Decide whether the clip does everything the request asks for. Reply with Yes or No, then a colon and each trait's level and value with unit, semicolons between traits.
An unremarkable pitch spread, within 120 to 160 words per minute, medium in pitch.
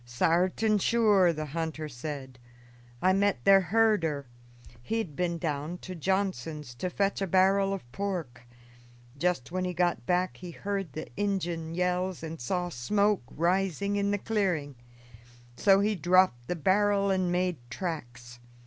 Yes: average, 4.0 semitones; average, 150 wpm; medium, 180 Hz